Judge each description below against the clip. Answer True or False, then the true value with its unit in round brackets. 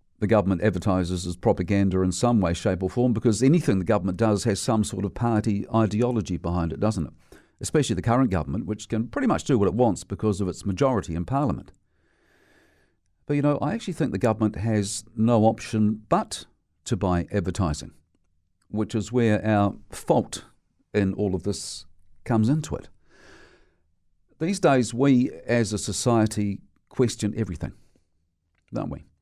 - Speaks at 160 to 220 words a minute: True (165 wpm)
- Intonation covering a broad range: False (4.0 semitones)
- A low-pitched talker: True (105 Hz)